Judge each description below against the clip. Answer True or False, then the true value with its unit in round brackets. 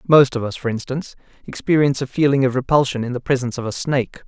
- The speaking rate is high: True (225 wpm)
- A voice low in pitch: True (130 Hz)